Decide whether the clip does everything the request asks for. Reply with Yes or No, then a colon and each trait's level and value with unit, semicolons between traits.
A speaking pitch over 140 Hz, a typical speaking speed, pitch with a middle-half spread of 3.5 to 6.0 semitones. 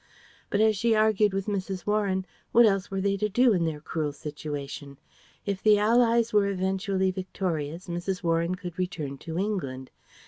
Yes: high, 190 Hz; average, 170 wpm; average, 3.8 semitones